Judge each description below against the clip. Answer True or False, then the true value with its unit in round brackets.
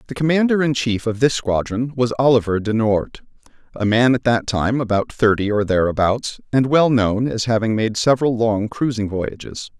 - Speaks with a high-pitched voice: False (115 Hz)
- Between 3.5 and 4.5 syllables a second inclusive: False (5.0 syllables/s)